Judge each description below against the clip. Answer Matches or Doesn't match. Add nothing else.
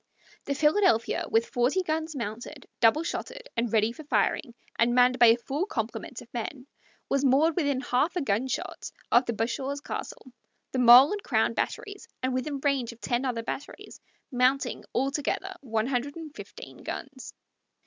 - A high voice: Matches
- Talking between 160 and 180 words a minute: Matches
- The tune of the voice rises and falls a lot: Doesn't match